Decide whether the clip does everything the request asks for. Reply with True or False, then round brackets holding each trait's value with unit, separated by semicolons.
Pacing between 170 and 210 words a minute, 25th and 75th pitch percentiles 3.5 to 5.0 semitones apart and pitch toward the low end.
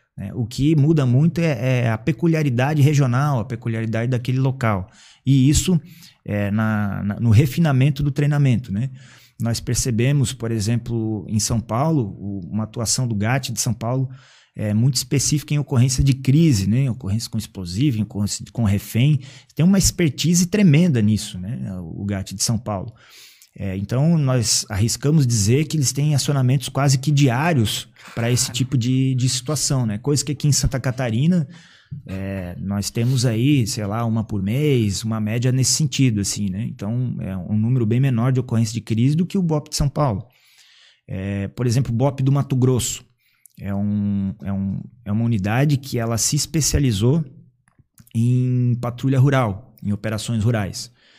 True (175 wpm; 4.2 semitones; 125 Hz)